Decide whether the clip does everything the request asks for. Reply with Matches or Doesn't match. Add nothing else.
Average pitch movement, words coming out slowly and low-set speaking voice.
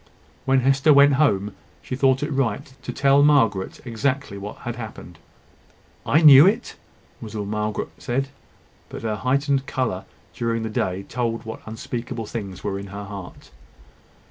Doesn't match